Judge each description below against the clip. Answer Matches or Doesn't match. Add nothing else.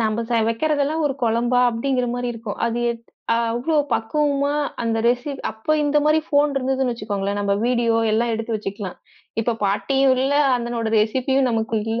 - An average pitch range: Matches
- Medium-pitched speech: Doesn't match